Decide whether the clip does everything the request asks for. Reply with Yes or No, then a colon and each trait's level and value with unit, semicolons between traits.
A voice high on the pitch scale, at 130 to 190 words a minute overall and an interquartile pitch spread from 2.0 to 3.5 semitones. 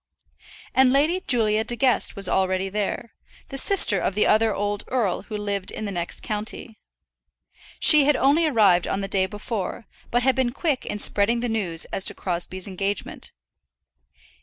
No: high, 215 Hz; average, 170 wpm; average, 4.2 semitones